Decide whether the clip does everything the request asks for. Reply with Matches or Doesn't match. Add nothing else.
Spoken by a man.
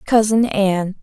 Doesn't match